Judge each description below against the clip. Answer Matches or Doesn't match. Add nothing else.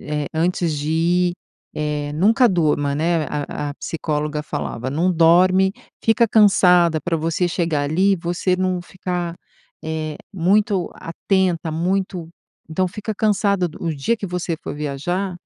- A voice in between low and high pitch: Matches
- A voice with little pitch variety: Doesn't match